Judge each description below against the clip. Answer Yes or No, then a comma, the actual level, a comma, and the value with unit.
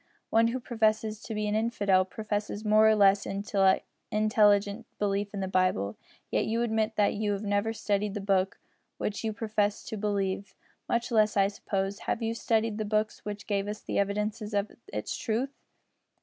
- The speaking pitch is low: No, high, 210 Hz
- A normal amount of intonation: No, narrow, 1.5 semitones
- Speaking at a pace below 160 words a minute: No, average, 175 wpm